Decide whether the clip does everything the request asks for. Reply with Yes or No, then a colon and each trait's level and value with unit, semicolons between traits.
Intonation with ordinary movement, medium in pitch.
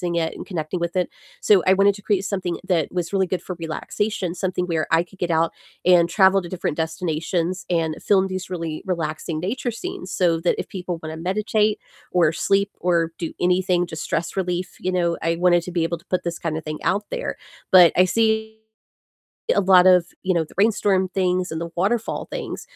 No: narrow, 2.3 semitones; medium, 180 Hz